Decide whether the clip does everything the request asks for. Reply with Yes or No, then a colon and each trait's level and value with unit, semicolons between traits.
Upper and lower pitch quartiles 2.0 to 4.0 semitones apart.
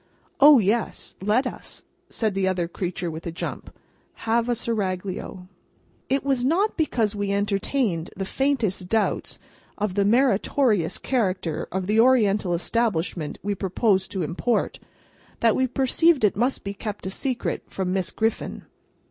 No: average, 4.6 semitones